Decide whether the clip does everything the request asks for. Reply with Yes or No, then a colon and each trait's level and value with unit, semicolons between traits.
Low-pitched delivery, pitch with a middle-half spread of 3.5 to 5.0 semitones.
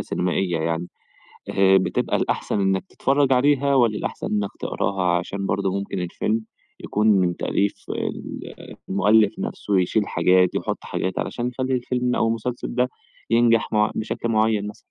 Yes: low, 105 Hz; average, 3.9 semitones